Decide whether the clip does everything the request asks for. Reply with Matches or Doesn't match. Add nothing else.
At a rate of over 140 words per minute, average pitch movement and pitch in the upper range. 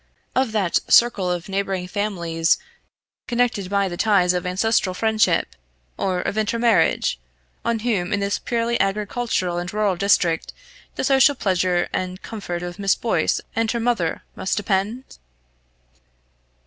Doesn't match